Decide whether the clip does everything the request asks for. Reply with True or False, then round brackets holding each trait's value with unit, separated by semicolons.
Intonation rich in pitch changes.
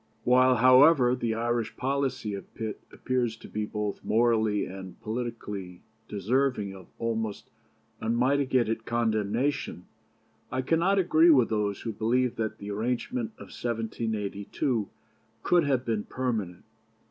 False (3.2 semitones)